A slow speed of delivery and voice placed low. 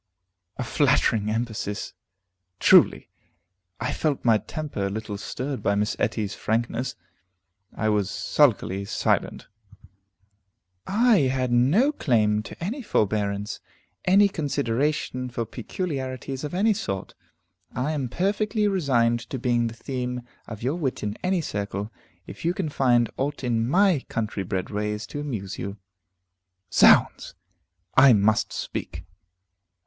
Yes: slow, 130 wpm; low, 125 Hz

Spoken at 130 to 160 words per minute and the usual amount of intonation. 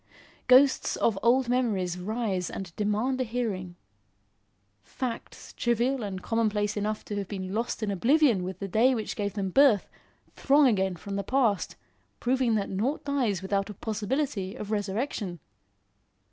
Yes: average, 150 wpm; average, 4.1 semitones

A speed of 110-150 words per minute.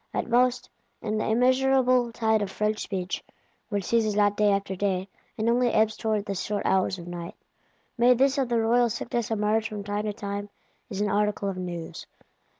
No: average, 190 wpm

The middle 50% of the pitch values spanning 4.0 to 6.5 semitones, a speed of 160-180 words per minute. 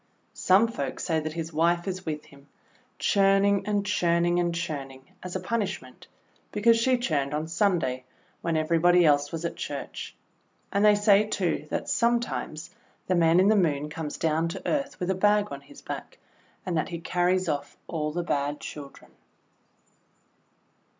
Yes: average, 4.4 semitones; average, 165 wpm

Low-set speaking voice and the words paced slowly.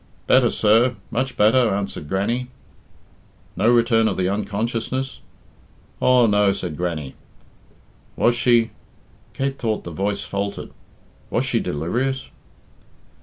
Yes: low, 110 Hz; slow, 115 wpm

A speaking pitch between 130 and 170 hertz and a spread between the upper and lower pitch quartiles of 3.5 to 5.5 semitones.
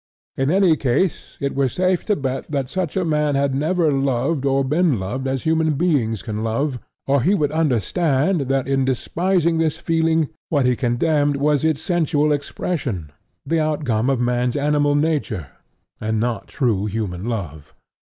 Yes: medium, 140 Hz; average, 4.4 semitones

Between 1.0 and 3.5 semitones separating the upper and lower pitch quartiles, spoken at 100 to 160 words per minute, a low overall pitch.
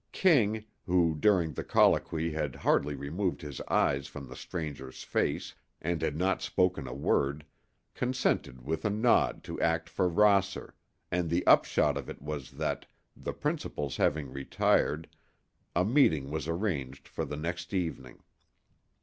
No: average, 4.3 semitones; average, 150 wpm; very low, 80 Hz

